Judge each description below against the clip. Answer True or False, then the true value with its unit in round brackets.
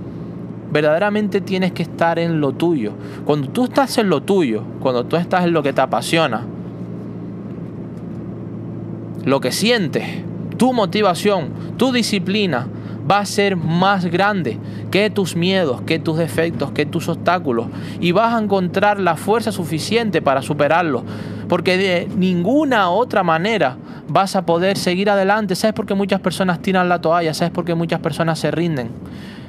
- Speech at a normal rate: True (155 wpm)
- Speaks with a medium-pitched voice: True (175 Hz)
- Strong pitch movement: False (4.1 semitones)